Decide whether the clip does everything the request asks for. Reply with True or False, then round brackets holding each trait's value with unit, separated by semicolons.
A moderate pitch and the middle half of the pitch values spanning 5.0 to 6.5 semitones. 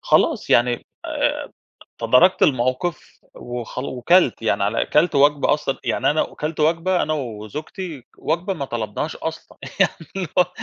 True (145 Hz; 5.6 semitones)